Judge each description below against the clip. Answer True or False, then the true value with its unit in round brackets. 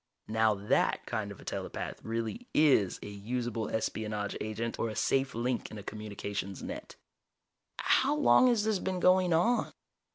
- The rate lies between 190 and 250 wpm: False (160 wpm)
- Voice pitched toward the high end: False (115 Hz)